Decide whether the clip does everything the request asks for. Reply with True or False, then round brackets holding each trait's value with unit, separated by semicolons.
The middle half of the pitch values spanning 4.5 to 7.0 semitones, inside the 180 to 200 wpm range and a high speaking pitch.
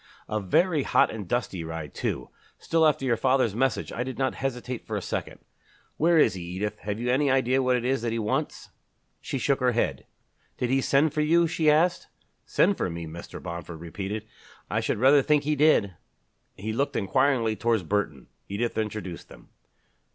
False (5.1 semitones; 190 wpm; 120 Hz)